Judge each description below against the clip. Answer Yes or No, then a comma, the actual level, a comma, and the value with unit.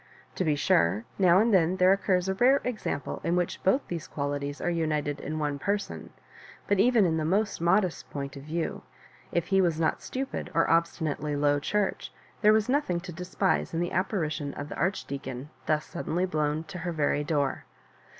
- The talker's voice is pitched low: No, medium, 170 Hz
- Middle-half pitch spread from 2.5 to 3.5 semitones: No, average, 4.3 semitones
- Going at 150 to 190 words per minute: No, average, 200 wpm